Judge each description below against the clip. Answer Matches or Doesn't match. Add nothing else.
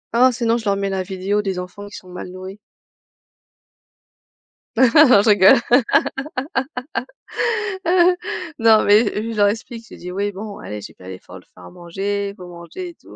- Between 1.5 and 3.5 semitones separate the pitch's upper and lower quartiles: Doesn't match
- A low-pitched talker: Doesn't match